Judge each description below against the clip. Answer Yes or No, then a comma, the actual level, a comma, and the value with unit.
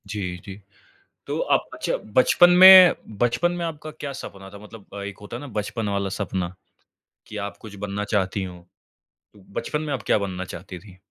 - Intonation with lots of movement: Yes, wide, 6.2 semitones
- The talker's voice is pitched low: Yes, low, 105 Hz